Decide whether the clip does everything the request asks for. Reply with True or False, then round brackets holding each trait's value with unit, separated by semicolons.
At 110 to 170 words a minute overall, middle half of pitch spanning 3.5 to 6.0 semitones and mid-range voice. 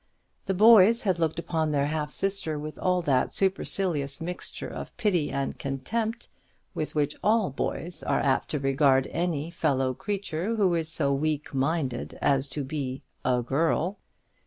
True (160 wpm; 4.8 semitones; 155 Hz)